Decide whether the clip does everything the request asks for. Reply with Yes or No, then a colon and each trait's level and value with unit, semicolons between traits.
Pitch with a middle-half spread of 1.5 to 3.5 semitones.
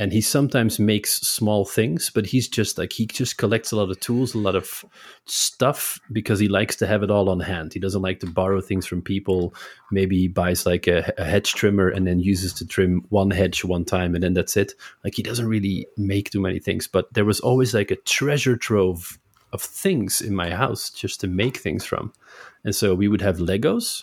Yes: average, 2.8 semitones